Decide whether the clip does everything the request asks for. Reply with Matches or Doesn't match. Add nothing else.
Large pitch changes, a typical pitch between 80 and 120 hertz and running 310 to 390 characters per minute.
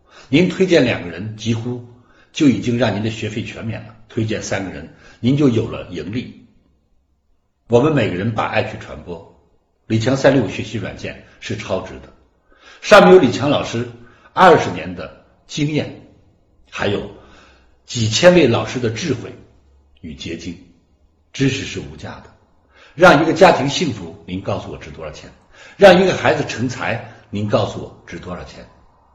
Doesn't match